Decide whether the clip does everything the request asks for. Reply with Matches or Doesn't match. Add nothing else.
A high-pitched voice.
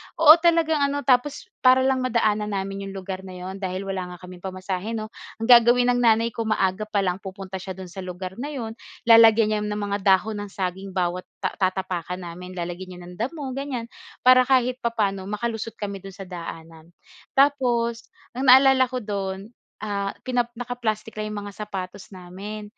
Matches